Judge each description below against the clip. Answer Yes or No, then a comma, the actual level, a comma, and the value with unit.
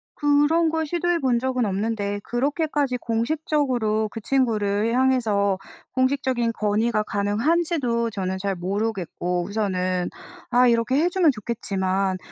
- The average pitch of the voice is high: Yes, high, 230 Hz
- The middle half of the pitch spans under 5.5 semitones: Yes, average, 5.1 semitones